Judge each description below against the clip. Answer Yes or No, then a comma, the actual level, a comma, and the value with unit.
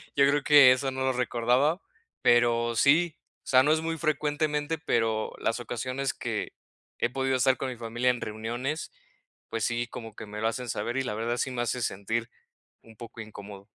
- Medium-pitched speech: No, low, 125 Hz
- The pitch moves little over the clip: No, average, 3.1 semitones